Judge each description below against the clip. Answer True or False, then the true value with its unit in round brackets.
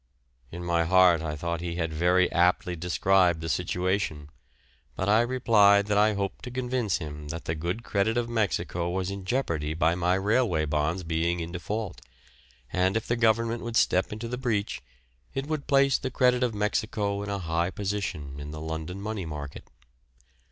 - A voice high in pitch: False (95 Hz)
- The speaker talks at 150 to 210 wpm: True (180 wpm)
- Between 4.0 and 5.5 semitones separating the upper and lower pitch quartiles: True (4.6 semitones)